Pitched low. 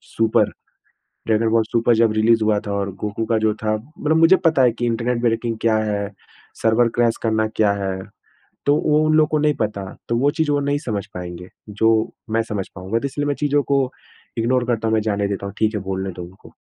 Yes: low, 115 Hz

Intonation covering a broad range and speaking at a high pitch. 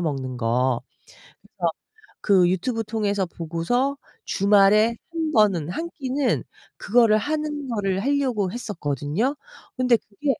Yes: wide, 6.5 semitones; high, 210 Hz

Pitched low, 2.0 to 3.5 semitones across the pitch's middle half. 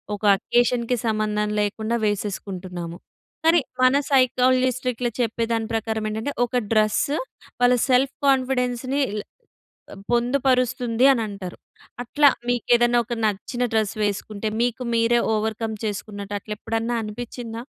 No: high, 230 Hz; average, 2.8 semitones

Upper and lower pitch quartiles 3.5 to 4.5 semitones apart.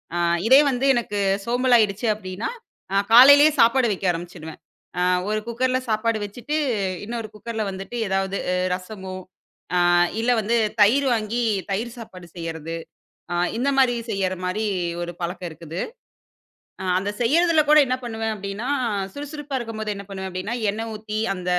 Yes: average, 4.1 semitones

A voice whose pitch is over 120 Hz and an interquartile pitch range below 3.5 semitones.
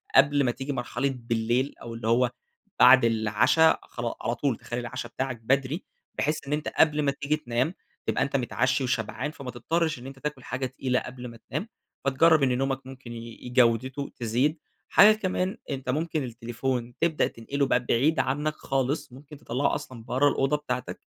Yes: low, 130 Hz; average, 3.0 semitones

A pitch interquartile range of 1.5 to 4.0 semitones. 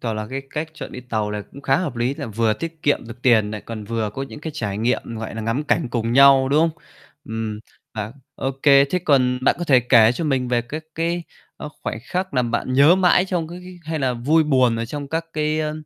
No: average, 5.1 semitones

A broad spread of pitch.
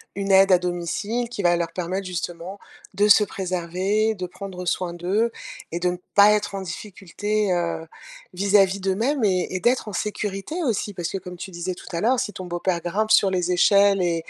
No: average, 2.7 semitones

